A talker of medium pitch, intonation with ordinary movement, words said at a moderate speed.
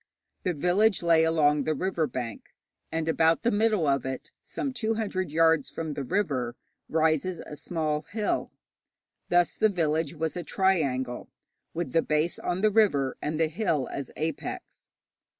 Yes: medium, 160 Hz; average, 3.7 semitones; average, 160 wpm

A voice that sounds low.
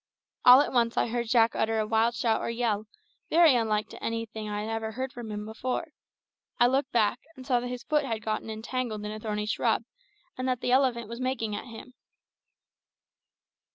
No: high, 230 Hz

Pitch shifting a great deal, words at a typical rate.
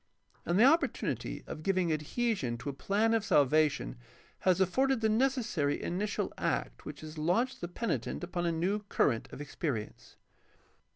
Yes: wide, 6.4 semitones; average, 155 wpm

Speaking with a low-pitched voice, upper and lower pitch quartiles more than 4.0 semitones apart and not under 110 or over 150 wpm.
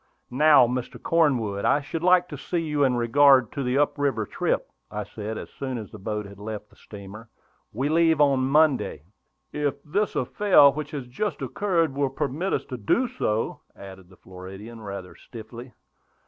No: low, 130 Hz; wide, 5.6 semitones; average, 180 wpm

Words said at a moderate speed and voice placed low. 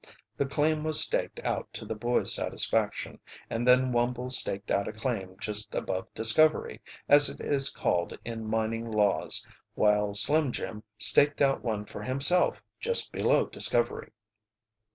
Yes: average, 150 wpm; low, 120 Hz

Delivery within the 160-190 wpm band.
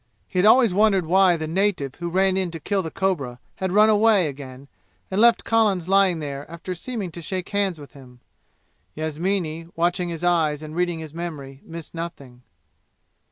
Yes: average, 180 wpm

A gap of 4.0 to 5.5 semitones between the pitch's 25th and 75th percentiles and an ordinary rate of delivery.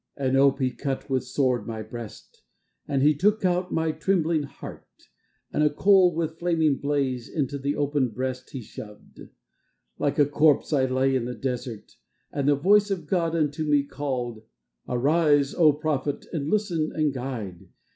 No: average, 3.4 semitones; average, 165 wpm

